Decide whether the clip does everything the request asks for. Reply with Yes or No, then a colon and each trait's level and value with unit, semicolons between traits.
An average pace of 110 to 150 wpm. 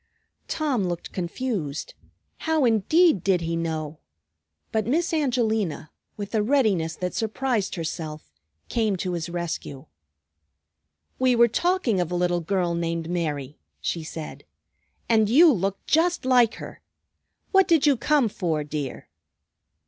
Yes: slow, 135 wpm